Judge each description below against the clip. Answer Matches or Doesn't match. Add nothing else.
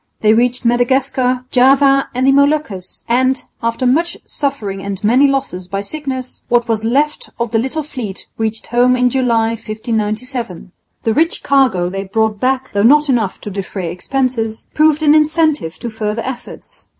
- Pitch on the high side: Matches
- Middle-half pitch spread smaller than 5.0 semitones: Matches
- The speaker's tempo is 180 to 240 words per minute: Doesn't match